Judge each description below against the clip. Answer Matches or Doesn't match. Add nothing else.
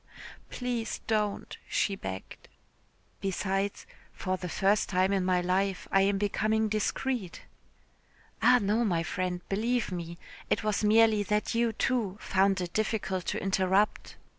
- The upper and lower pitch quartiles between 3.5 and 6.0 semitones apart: Doesn't match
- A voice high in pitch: Matches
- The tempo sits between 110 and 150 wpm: Matches